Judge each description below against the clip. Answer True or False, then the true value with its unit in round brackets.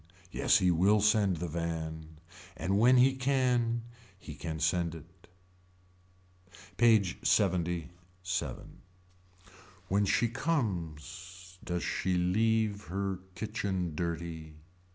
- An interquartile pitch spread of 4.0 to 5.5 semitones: True (4.3 semitones)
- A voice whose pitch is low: True (95 Hz)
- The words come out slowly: True (100 wpm)